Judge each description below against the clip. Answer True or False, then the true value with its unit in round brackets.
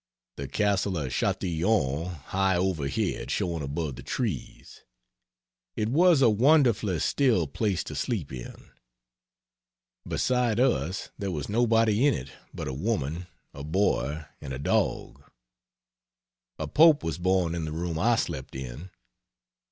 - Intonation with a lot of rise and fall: True (6.8 semitones)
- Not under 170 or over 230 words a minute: False (135 wpm)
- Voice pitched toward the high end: False (90 Hz)